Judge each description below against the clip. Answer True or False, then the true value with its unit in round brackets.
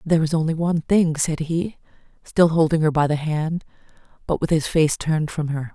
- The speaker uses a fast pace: True (210 wpm)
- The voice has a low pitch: False (160 Hz)